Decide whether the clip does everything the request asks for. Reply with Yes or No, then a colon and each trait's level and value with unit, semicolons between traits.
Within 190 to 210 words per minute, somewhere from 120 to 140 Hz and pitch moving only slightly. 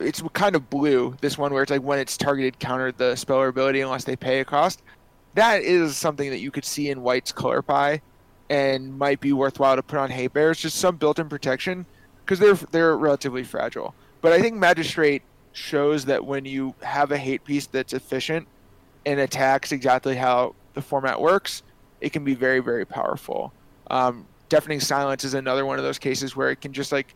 Yes: fast, 205 wpm; low, 135 Hz; narrow, 2.0 semitones